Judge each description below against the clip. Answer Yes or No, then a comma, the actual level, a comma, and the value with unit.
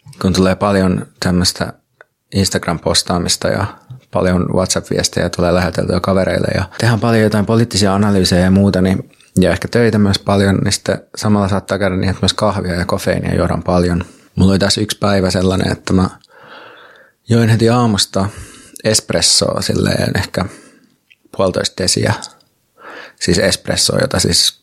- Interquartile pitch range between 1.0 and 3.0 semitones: Yes, narrow, 2.6 semitones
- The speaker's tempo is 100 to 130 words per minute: No, average, 140 wpm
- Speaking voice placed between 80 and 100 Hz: Yes, very low, 95 Hz